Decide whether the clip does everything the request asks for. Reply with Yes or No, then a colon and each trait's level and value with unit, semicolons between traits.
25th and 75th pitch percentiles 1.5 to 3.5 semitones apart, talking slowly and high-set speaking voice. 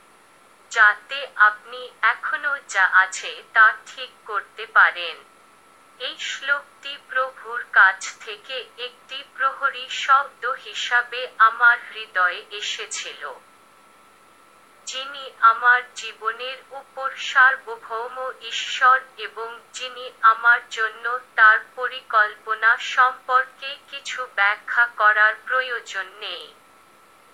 Yes: average, 3.2 semitones; slow, 85 wpm; high, 240 Hz